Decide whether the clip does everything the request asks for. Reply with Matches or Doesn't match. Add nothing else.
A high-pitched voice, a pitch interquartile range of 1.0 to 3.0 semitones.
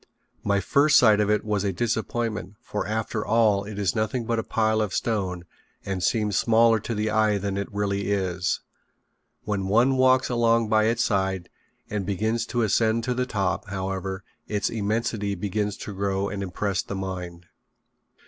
Doesn't match